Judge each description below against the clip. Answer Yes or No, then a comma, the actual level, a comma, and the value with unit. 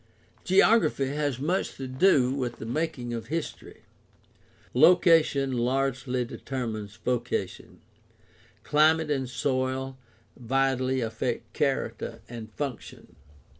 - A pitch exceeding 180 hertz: No, low, 130 Hz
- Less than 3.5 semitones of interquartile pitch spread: Yes, average, 3.1 semitones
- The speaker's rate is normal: No, slow, 100 wpm